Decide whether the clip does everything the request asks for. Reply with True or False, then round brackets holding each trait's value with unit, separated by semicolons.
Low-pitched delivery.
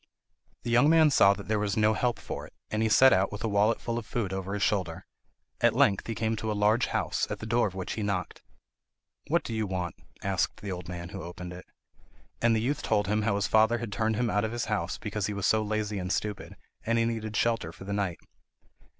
True (105 Hz)